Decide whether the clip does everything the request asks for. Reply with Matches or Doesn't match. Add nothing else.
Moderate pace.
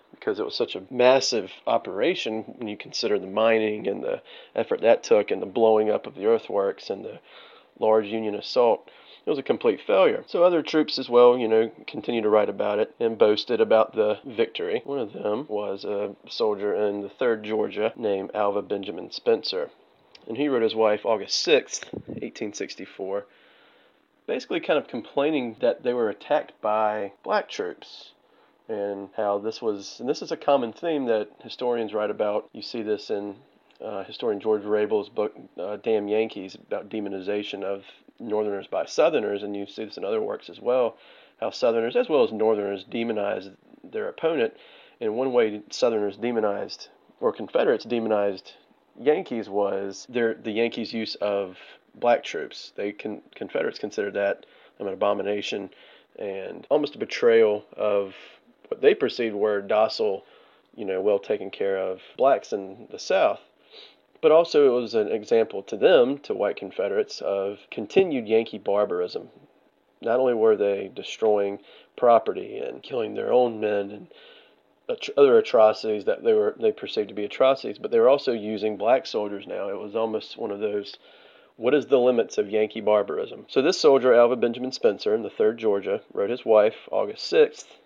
Matches